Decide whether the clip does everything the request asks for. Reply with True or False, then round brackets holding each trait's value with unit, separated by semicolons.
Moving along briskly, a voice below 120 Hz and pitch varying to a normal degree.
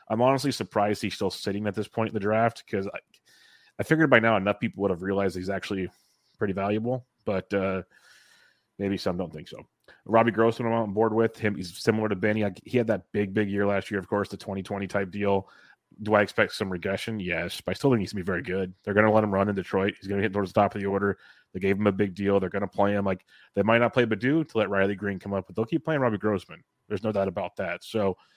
False (270 wpm; 100 Hz; 2.2 semitones)